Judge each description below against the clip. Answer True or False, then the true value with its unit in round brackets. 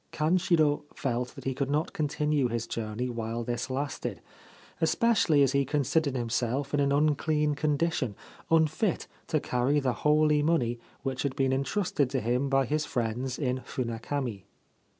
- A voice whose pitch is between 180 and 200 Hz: False (140 Hz)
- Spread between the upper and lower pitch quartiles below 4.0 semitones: True (3.4 semitones)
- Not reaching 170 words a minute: True (150 wpm)